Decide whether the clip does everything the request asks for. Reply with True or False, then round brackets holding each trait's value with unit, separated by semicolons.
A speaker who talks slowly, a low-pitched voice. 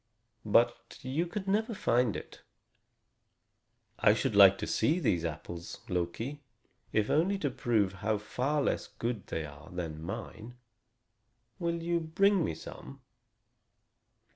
True (130 wpm; 120 Hz)